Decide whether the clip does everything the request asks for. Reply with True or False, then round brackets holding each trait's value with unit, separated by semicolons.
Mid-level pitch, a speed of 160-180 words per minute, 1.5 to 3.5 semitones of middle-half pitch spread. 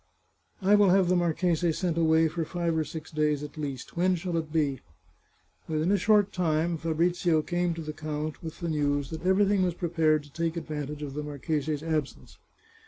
False (160 Hz; 200 wpm; 2.4 semitones)